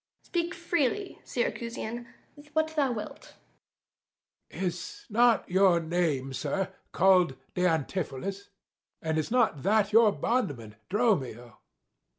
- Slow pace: Yes, slow, 120 wpm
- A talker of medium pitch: No, high, 195 Hz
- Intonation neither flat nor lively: No, wide, 6.9 semitones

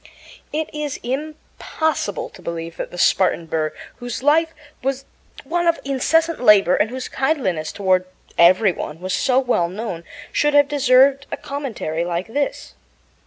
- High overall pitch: Yes, very high, 255 Hz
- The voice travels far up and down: Yes, wide, 8.0 semitones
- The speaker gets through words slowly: No, average, 150 wpm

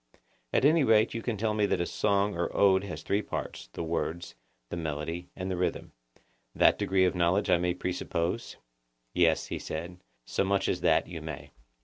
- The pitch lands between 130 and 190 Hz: No, very low, 90 Hz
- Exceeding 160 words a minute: Yes, average, 185 wpm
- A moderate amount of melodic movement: Yes, average, 3.0 semitones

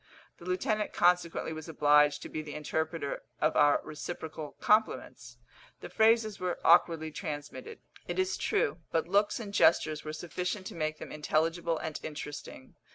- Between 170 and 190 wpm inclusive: No, average, 155 wpm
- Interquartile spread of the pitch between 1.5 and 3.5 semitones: Yes, average, 3.2 semitones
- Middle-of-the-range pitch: Yes, medium, 160 Hz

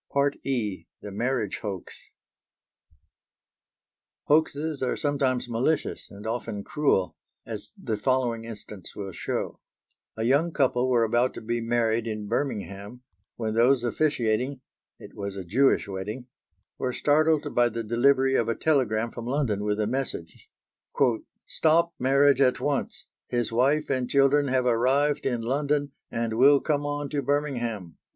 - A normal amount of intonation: Yes, average, 4.0 semitones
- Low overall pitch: Yes, low, 125 Hz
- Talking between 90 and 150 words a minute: Yes, average, 140 wpm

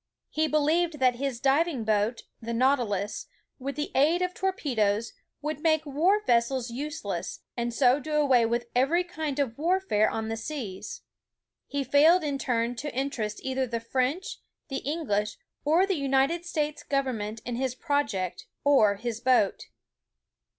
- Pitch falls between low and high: No, very high, 270 Hz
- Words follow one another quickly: No, average, 155 wpm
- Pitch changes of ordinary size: Yes, average, 4.6 semitones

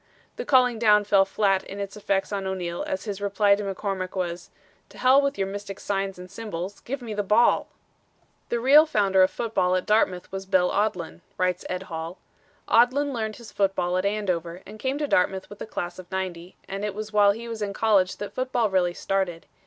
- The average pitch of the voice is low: No, high, 200 Hz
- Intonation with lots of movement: No, average, 2.7 semitones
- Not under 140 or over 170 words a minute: No, fast, 205 wpm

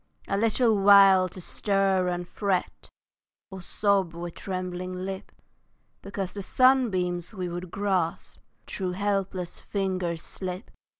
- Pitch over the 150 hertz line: Yes, high, 190 Hz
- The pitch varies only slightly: Yes, narrow, 1.8 semitones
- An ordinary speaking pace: No, slow, 120 wpm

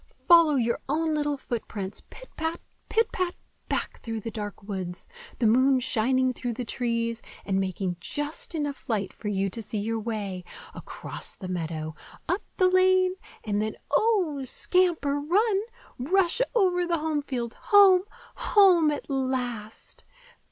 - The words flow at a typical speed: Yes, average, 145 wpm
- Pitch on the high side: Yes, very high, 265 Hz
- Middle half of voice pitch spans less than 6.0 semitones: No, wide, 8.1 semitones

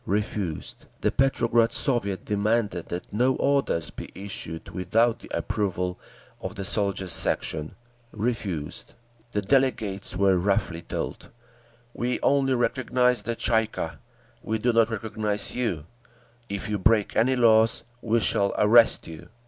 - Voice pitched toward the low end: Yes, low, 105 Hz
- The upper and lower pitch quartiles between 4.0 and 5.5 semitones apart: No, average, 3.5 semitones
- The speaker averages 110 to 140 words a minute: Yes, slow, 135 wpm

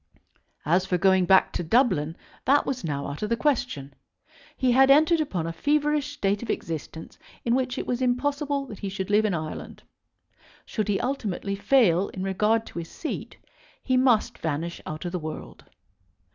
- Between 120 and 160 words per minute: No, average, 180 wpm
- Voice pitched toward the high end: Yes, high, 210 Hz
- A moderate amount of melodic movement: No, wide, 7.3 semitones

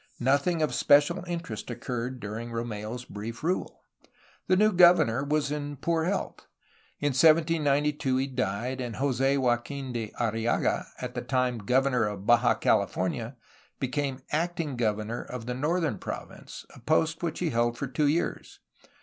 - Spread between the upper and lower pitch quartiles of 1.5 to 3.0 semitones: No, average, 4.3 semitones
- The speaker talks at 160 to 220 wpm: No, average, 150 wpm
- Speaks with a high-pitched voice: No, low, 130 Hz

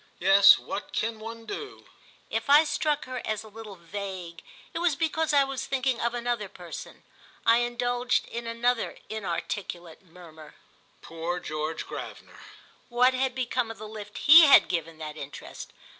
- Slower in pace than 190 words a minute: Yes, average, 155 wpm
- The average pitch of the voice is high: Yes, high, 225 Hz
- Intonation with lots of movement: Yes, wide, 5.9 semitones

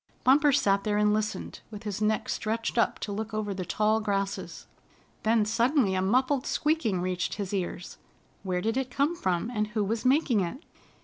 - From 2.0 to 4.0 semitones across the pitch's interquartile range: Yes, average, 3.6 semitones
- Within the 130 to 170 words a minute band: No, average, 185 wpm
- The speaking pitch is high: Yes, high, 215 Hz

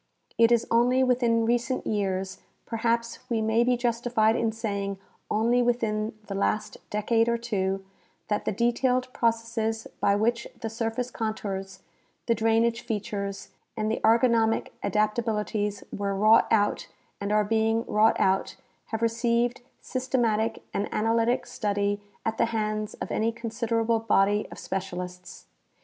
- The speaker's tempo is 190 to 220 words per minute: No, average, 140 wpm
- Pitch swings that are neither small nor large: No, narrow, 2.0 semitones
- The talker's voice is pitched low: No, high, 225 Hz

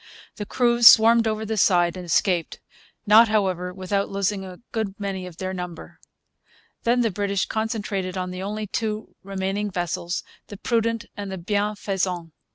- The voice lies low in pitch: No, high, 200 Hz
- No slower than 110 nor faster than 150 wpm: No, average, 160 wpm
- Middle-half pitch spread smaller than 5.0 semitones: Yes, average, 2.8 semitones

